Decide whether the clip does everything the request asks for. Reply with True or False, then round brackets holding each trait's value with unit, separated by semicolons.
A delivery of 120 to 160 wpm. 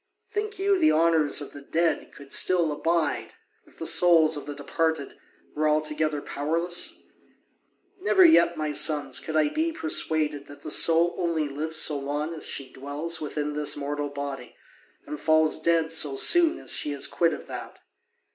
False (170 wpm)